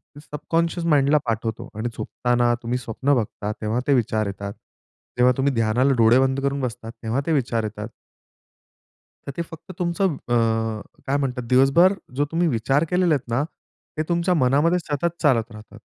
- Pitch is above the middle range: No, low, 130 Hz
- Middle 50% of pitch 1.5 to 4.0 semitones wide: No, average, 4.8 semitones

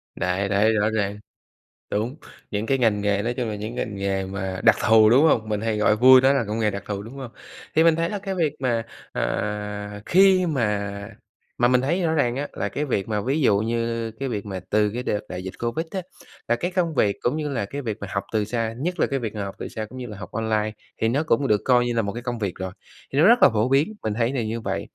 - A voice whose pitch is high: No, low, 115 Hz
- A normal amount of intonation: Yes, average, 4.5 semitones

